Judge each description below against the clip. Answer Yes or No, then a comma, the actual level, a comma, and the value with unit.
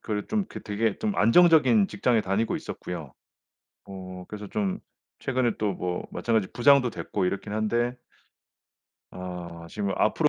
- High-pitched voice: No, low, 105 Hz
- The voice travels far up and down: No, average, 4.5 semitones